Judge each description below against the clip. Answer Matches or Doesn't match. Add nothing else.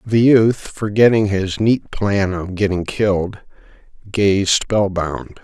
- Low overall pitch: Matches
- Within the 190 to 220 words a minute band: Doesn't match